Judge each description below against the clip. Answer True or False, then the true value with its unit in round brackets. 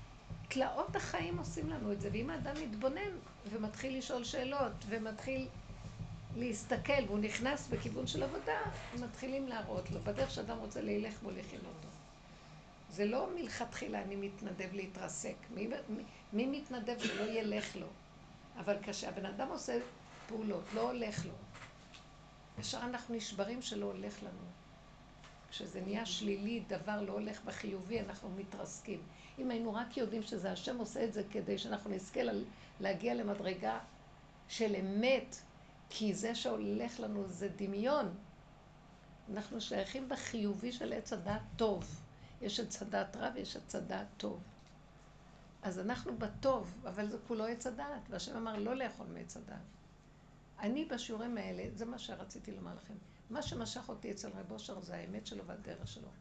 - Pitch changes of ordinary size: True (3.9 semitones)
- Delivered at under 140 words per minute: False (145 wpm)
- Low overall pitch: False (210 Hz)